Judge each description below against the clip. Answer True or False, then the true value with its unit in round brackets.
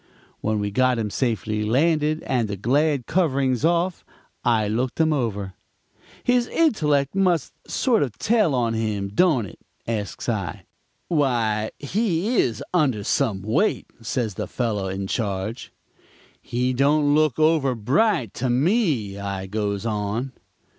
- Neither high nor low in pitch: False (125 Hz)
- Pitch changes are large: True (6.4 semitones)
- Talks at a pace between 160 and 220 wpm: False (140 wpm)